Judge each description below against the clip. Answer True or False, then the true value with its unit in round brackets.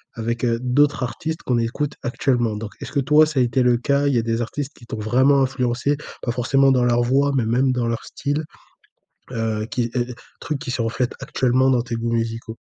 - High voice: False (125 Hz)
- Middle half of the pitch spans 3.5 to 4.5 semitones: False (2.7 semitones)